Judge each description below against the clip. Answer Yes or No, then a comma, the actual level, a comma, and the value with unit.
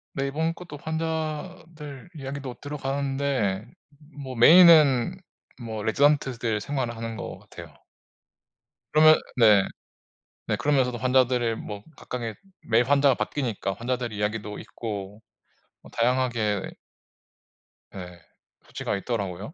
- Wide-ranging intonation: No, average, 4.4 semitones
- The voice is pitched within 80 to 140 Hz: Yes, low, 125 Hz